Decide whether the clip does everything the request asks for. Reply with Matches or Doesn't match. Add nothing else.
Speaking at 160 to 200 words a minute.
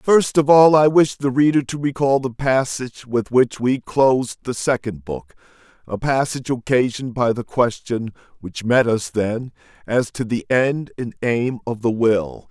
Matches